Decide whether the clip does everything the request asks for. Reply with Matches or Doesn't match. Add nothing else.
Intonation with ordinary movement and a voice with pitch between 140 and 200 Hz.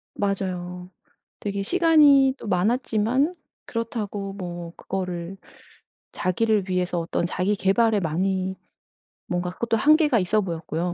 Matches